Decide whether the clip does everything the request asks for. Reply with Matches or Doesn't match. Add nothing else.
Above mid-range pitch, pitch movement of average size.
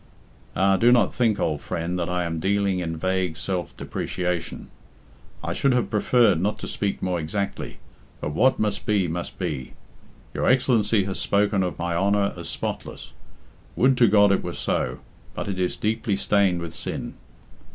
Doesn't match